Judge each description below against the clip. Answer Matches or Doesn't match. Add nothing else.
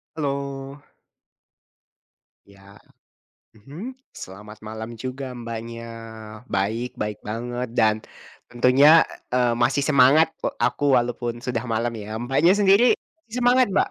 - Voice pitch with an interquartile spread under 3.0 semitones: Doesn't match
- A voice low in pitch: Matches